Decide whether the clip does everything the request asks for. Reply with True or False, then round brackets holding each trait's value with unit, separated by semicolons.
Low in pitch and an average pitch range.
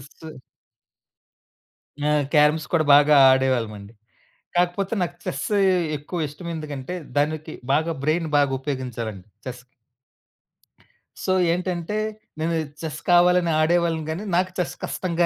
False (155 Hz; 3.7 semitones)